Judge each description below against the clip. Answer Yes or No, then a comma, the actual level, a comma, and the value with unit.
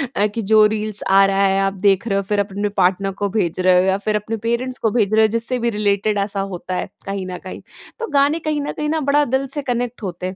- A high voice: Yes, high, 205 Hz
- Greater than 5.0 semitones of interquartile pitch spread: No, average, 3.3 semitones